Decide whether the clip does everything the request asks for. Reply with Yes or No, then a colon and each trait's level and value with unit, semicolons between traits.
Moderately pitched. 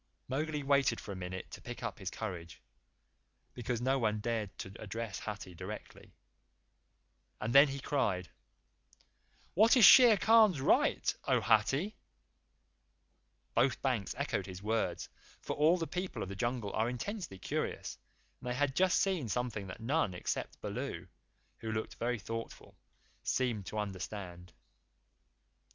No: low, 115 Hz